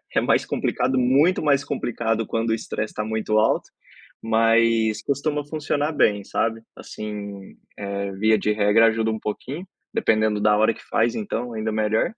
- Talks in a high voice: No, low, 110 Hz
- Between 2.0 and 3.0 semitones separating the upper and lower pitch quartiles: Yes, narrow, 2.4 semitones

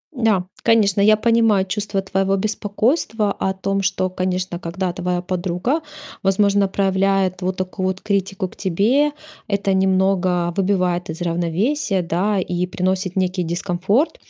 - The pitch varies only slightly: Yes, narrow, 1.9 semitones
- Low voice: No, high, 190 Hz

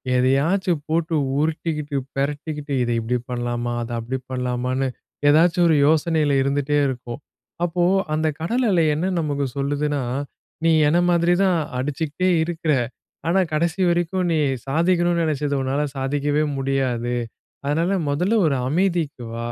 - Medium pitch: Yes, medium, 150 Hz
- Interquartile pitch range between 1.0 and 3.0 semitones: No, average, 3.7 semitones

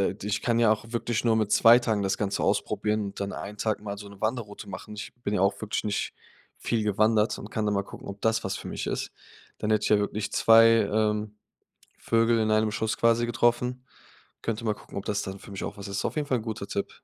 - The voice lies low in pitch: Yes, low, 110 Hz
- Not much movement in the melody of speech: Yes, narrow, 1.9 semitones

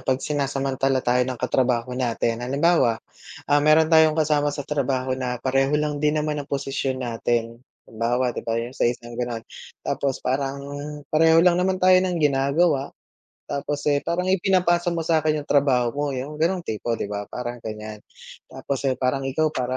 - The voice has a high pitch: No, low, 135 Hz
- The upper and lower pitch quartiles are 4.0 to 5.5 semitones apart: No, average, 3.6 semitones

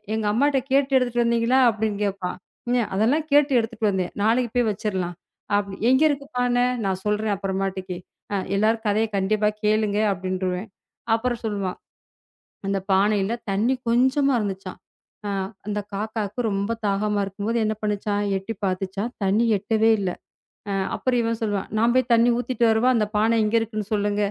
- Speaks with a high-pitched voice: Yes, high, 215 Hz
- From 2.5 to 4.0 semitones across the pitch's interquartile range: Yes, average, 2.9 semitones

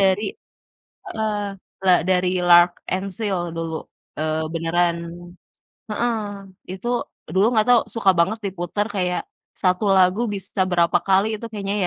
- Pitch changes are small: No, average, 3.1 semitones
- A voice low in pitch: No, high, 190 Hz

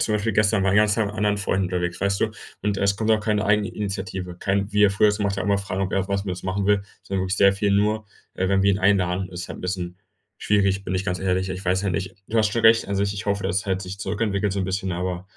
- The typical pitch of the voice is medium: No, low, 100 Hz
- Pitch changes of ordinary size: No, narrow, 1.7 semitones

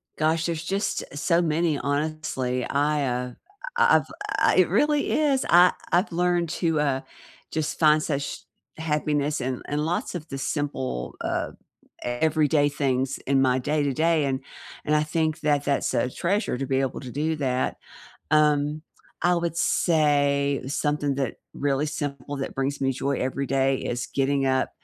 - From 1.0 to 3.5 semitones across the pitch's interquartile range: Yes, average, 2.8 semitones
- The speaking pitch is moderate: Yes, medium, 145 Hz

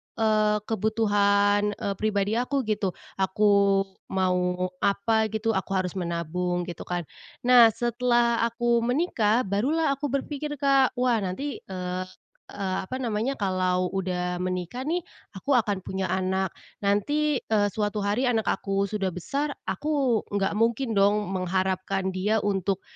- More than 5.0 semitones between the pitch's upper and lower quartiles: No, average, 4.0 semitones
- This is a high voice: Yes, high, 205 Hz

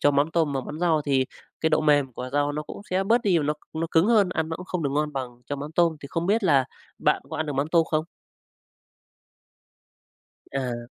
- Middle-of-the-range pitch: Yes, medium, 150 Hz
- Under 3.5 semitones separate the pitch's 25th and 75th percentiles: Yes, average, 3.0 semitones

